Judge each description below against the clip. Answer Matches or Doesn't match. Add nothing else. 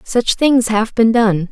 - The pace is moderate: Matches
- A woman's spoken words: Matches